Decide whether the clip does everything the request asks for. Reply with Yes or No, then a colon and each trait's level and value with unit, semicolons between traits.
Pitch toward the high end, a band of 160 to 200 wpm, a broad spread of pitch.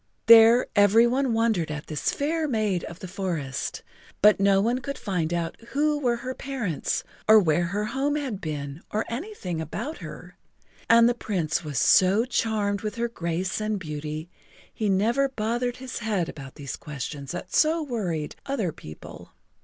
Yes: high, 210 Hz; average, 170 wpm; wide, 6.2 semitones